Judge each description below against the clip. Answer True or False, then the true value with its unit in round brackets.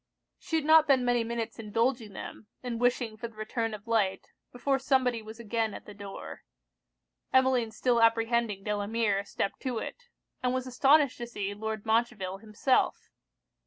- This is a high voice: True (230 Hz)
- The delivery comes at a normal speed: True (160 wpm)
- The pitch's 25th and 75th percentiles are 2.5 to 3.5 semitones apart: True (2.8 semitones)